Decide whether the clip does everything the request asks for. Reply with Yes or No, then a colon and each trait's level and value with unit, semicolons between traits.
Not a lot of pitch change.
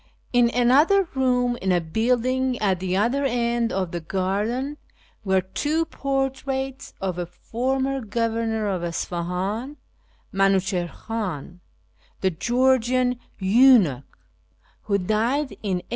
No: wide, 5.5 semitones